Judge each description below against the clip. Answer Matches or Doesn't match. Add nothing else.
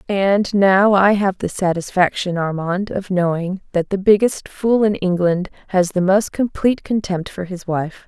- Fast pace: Doesn't match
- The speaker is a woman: Matches